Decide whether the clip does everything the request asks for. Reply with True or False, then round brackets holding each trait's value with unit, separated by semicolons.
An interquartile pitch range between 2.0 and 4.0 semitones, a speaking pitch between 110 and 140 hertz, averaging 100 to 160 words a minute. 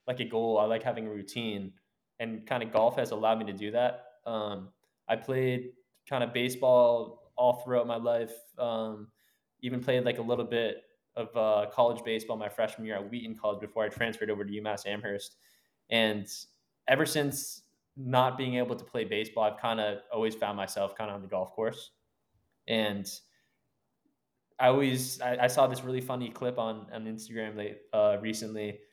False (2.8 semitones; 115 Hz; 185 wpm)